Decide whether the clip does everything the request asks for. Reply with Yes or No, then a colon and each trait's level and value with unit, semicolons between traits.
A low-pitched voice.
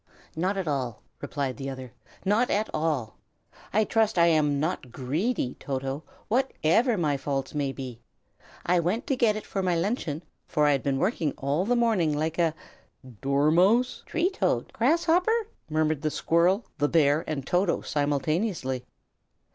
No: medium, 160 Hz